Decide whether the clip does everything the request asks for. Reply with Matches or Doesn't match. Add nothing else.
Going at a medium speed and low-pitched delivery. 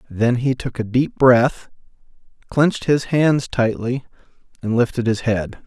Matches